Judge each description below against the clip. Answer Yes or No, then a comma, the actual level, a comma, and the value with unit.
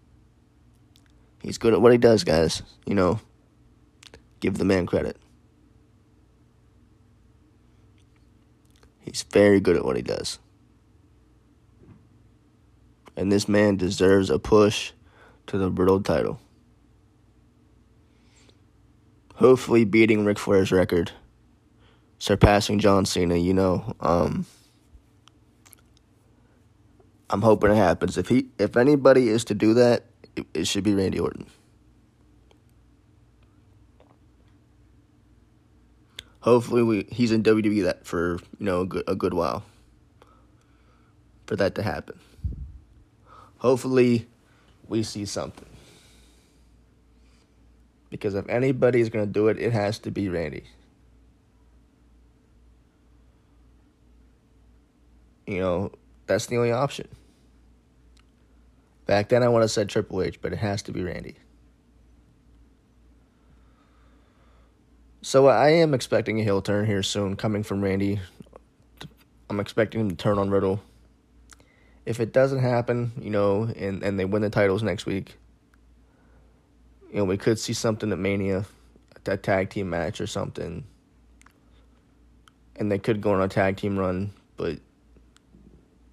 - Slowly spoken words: Yes, slow, 115 wpm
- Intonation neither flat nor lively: No, wide, 7.3 semitones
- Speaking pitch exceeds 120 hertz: No, low, 100 Hz